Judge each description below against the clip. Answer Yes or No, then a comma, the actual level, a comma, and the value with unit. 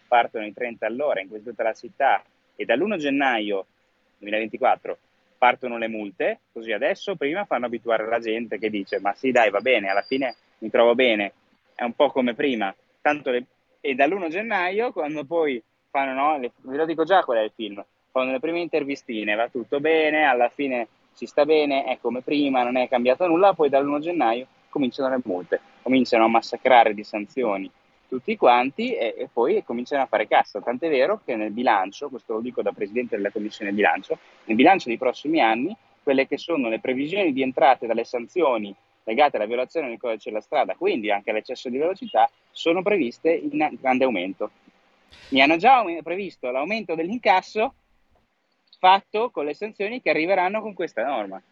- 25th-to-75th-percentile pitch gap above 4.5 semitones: Yes, wide, 5.6 semitones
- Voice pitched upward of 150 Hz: No, low, 130 Hz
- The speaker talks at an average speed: No, fast, 180 wpm